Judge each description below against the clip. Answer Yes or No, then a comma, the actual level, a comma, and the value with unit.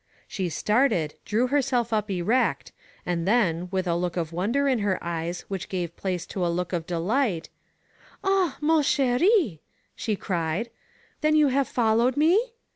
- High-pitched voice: Yes, high, 210 Hz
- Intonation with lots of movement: Yes, wide, 7.4 semitones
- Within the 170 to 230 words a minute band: No, average, 160 wpm